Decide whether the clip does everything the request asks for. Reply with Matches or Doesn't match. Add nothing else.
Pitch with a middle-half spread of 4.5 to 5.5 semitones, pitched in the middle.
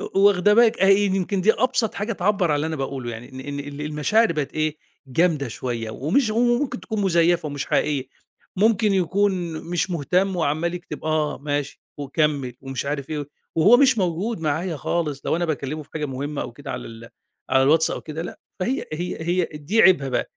Matches